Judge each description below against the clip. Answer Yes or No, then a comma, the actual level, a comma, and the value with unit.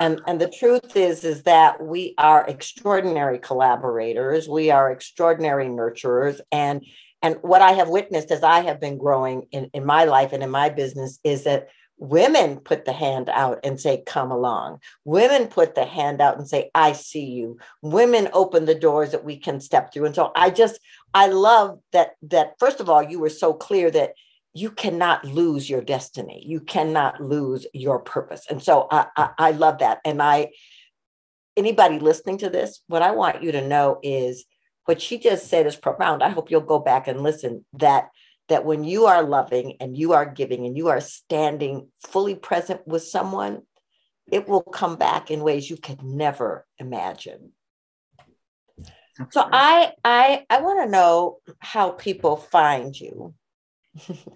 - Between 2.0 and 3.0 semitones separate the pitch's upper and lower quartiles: No, average, 4.6 semitones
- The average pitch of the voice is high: No, medium, 155 Hz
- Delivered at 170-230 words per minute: Yes, average, 180 wpm